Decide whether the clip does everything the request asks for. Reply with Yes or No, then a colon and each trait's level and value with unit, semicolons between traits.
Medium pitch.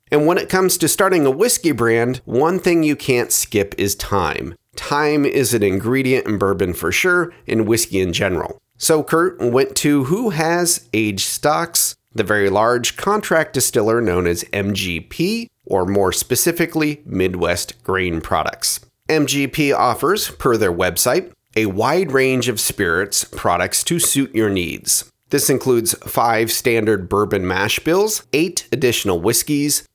No: low, 120 Hz